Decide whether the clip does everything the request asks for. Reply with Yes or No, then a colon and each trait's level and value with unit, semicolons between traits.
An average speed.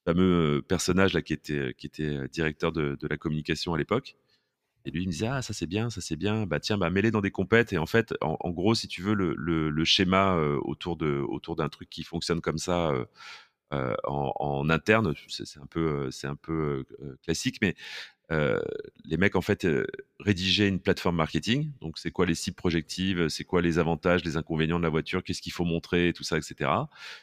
No: fast, 225 wpm